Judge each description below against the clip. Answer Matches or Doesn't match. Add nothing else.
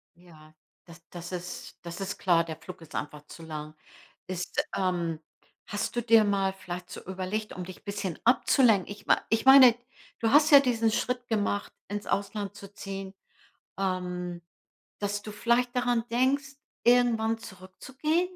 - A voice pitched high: Matches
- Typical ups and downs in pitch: Matches